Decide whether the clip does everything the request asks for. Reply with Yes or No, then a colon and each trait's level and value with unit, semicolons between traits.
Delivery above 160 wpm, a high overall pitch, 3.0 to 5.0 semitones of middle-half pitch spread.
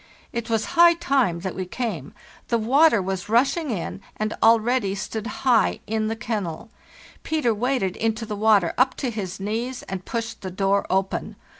Yes: average, 170 wpm; high, 220 Hz; average, 4.0 semitones